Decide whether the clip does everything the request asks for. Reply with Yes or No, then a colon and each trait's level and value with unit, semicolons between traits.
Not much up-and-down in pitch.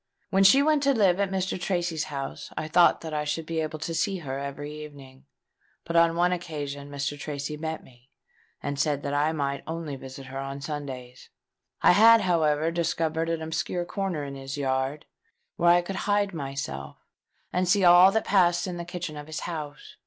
No: average, 3.7 semitones